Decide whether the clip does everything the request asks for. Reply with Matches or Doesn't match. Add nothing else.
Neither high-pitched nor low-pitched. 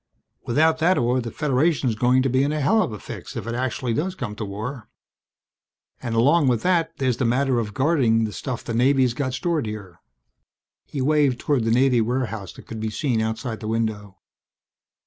Doesn't match